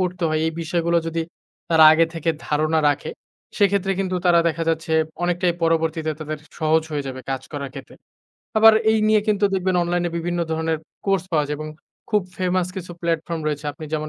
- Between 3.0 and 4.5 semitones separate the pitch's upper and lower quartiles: No, narrow, 2.6 semitones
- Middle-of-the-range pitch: Yes, medium, 165 Hz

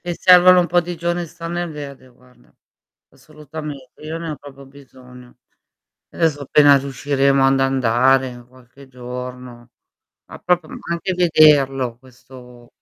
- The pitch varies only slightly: No, average, 4.0 semitones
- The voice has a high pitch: No, medium, 140 Hz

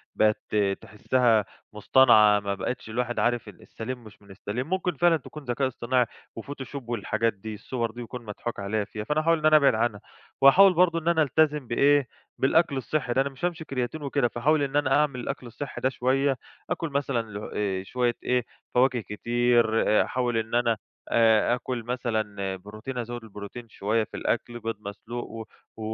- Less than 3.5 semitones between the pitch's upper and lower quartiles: No, average, 3.8 semitones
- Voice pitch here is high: No, low, 120 Hz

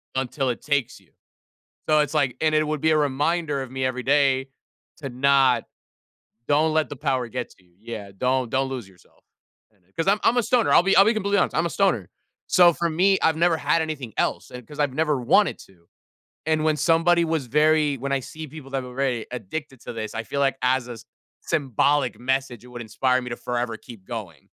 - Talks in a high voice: No, low, 135 Hz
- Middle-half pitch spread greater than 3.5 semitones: Yes, average, 4.1 semitones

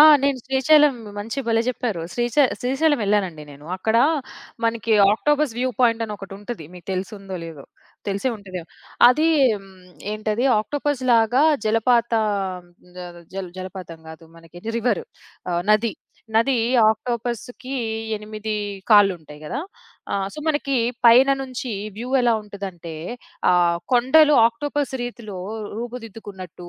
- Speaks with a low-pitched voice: No, high, 225 Hz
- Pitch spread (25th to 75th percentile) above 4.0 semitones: Yes, average, 4.5 semitones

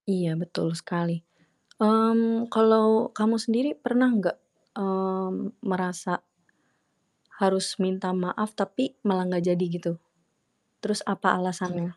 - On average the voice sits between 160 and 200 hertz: Yes, high, 190 Hz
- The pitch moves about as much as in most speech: Yes, average, 3.5 semitones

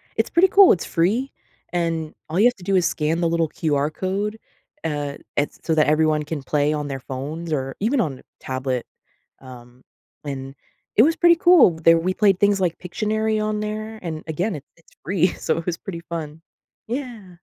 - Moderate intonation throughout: No, wide, 5.9 semitones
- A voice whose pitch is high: No, medium, 170 Hz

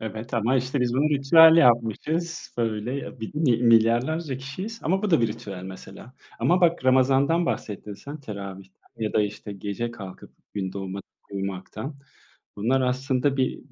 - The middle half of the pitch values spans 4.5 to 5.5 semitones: Yes, average, 5.0 semitones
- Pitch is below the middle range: Yes, low, 125 Hz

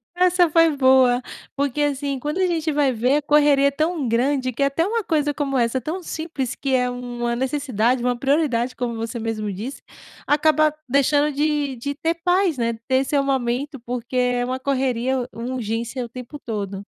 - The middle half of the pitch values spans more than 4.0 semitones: No, average, 3.3 semitones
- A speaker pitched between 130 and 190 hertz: No, very high, 265 Hz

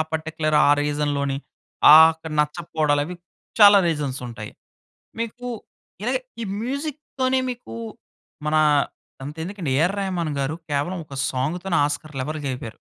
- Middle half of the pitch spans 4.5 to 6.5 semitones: Yes, average, 4.9 semitones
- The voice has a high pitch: No, medium, 160 Hz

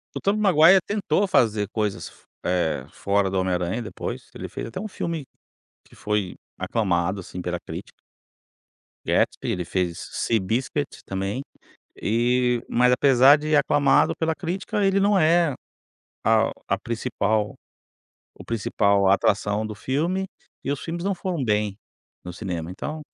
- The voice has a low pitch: Yes, low, 115 Hz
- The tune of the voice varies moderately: No, wide, 8.1 semitones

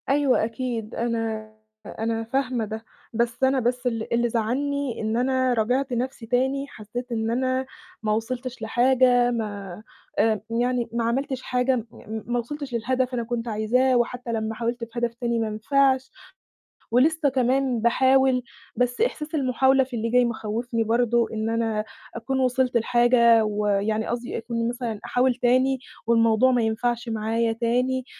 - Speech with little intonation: Yes, narrow, 2.2 semitones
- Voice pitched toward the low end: No, high, 240 Hz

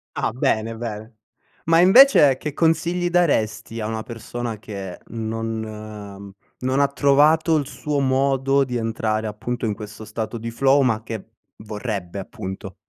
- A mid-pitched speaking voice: No, low, 115 Hz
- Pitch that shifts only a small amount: No, average, 4.3 semitones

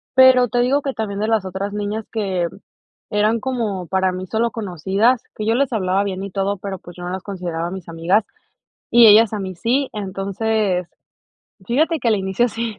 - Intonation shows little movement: No, average, 3.4 semitones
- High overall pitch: Yes, high, 205 Hz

